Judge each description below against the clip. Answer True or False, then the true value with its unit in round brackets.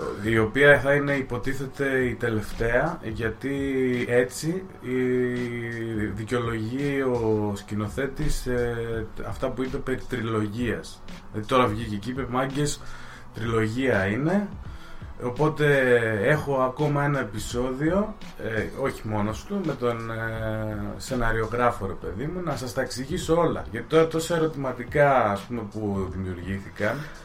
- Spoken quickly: False (120 wpm)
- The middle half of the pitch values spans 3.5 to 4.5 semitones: True (4.0 semitones)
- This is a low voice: True (125 Hz)